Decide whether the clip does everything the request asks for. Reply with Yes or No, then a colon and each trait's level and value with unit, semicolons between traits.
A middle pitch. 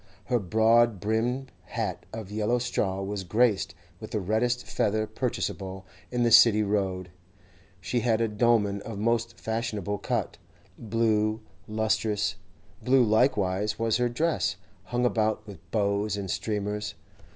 No: low, 110 Hz